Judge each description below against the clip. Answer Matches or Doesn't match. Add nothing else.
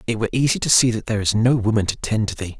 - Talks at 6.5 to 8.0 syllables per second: Matches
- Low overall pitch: Matches